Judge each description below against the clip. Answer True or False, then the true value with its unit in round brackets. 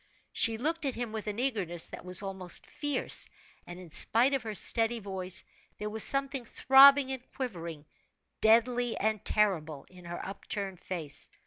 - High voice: True (215 Hz)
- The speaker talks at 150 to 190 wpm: True (160 wpm)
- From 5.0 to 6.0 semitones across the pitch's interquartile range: True (5.4 semitones)